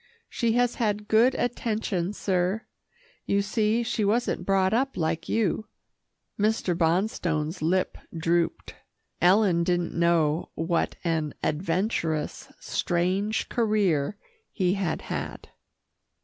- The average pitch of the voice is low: No, high, 190 Hz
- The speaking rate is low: Yes, slow, 105 wpm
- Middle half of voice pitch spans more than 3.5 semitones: Yes, average, 4.2 semitones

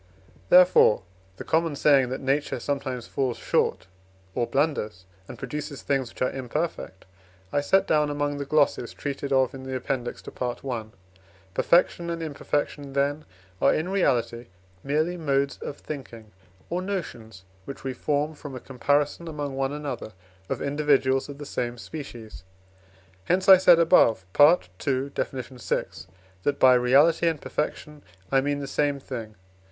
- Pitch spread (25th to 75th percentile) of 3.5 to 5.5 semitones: No, average, 2.8 semitones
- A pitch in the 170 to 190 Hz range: No, medium, 140 Hz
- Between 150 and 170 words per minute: Yes, average, 155 wpm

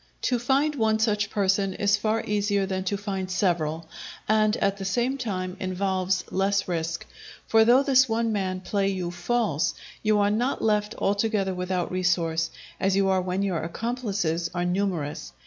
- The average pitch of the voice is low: No, high, 195 Hz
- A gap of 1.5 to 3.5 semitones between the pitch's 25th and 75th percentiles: Yes, average, 2.9 semitones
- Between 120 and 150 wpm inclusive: No, average, 165 wpm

